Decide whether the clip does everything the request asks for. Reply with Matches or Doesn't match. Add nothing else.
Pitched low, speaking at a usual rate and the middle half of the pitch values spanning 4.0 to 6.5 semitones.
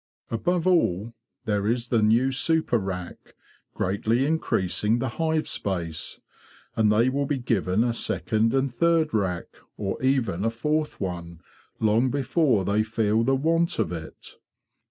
Matches